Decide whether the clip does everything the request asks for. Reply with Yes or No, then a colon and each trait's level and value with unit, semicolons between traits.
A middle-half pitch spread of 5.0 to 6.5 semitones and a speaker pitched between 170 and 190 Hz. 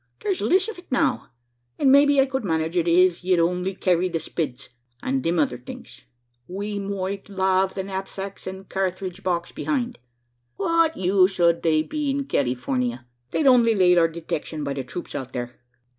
No: average, 3.7 semitones; medium, 185 Hz